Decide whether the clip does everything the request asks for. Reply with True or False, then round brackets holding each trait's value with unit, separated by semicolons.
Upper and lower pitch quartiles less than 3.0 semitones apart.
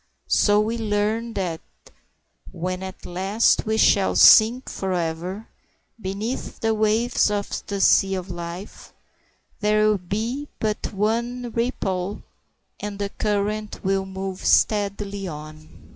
True (2.4 semitones)